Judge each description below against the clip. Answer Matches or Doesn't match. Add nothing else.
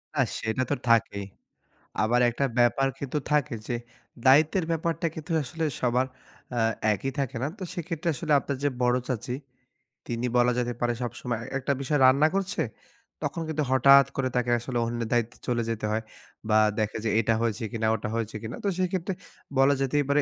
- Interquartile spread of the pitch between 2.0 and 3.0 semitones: Doesn't match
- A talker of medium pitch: Doesn't match